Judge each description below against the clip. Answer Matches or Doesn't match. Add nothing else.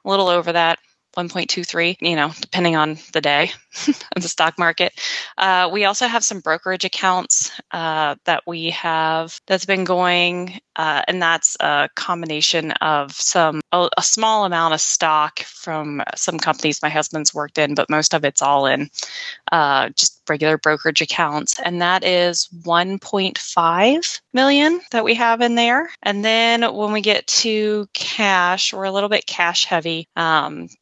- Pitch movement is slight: Doesn't match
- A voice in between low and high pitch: Matches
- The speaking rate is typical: Matches